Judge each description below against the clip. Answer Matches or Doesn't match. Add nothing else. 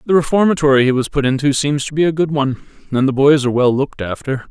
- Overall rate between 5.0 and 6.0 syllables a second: Doesn't match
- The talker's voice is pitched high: Doesn't match